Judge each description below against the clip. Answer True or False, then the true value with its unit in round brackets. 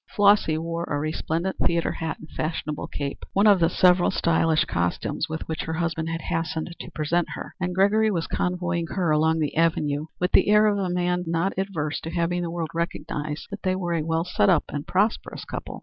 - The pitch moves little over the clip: True (2.3 semitones)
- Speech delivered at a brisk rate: True (210 wpm)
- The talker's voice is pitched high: False (170 Hz)